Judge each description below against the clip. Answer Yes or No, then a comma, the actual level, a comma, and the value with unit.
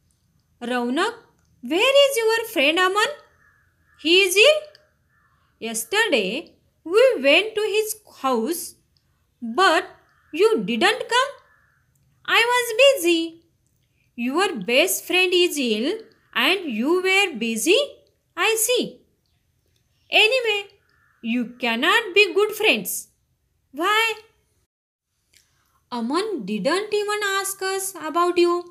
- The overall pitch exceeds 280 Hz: Yes, very high, 370 Hz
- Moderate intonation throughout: No, wide, 5.9 semitones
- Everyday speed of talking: Yes, average, 100 wpm